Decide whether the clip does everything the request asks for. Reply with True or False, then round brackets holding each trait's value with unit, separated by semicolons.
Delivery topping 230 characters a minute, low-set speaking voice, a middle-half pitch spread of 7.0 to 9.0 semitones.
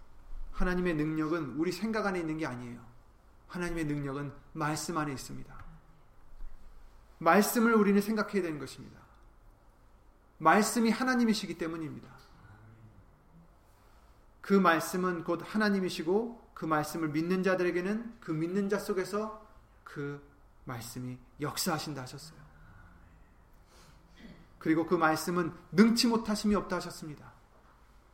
False (270 characters per minute; 160 Hz; 7.9 semitones)